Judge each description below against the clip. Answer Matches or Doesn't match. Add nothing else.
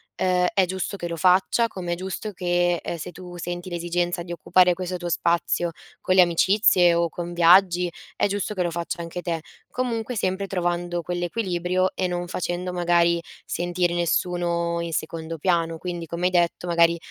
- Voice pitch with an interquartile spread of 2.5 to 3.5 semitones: Doesn't match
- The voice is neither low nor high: Matches